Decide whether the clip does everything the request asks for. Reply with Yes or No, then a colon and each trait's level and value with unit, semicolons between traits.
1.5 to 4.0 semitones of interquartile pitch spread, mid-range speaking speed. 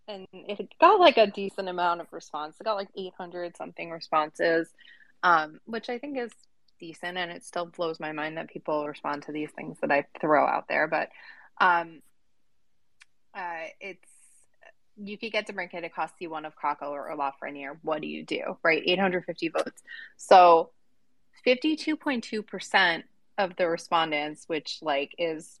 No: average, 4.6 semitones; average, 160 wpm